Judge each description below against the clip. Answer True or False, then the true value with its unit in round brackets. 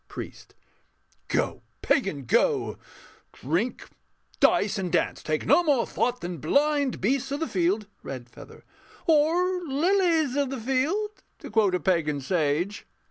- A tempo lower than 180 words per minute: True (135 wpm)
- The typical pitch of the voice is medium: False (240 Hz)